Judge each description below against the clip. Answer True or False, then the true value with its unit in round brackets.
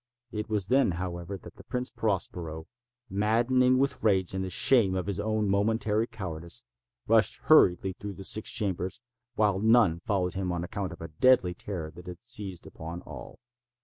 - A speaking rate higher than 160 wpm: True (175 wpm)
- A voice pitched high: False (95 Hz)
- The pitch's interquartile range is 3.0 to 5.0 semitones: True (3.6 semitones)